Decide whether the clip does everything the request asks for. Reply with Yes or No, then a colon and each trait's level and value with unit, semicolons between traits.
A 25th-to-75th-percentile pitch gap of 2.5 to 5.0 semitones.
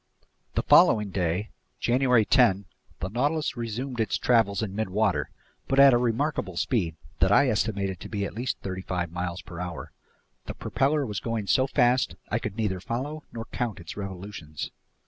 Yes: average, 4.6 semitones